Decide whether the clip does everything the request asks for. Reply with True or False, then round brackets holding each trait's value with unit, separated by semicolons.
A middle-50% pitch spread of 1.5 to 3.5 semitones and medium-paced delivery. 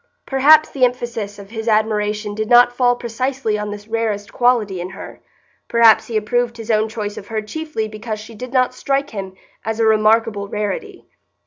True (2.6 semitones; 185 wpm)